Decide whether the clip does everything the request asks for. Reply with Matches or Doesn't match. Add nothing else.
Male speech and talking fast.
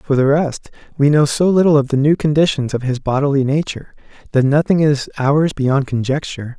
Doesn't match